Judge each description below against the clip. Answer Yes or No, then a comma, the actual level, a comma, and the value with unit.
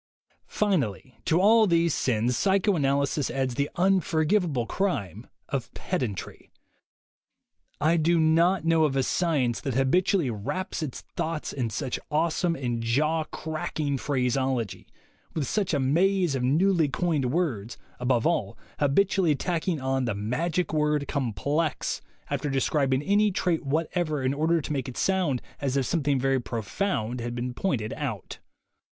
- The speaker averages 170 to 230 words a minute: No, average, 140 wpm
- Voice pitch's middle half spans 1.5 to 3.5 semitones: No, average, 4.9 semitones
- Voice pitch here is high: No, medium, 145 Hz